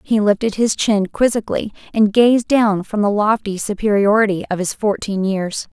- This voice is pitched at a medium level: No, high, 210 Hz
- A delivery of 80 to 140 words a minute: No, average, 165 wpm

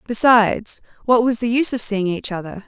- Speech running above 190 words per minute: Yes, average, 200 wpm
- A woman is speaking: Yes, female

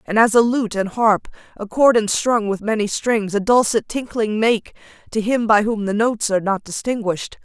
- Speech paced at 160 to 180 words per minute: No, average, 195 wpm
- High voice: Yes, high, 215 Hz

